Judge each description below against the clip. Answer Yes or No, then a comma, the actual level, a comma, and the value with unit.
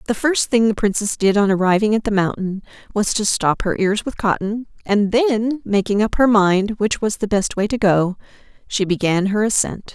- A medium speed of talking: No, fast, 210 wpm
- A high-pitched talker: Yes, high, 210 Hz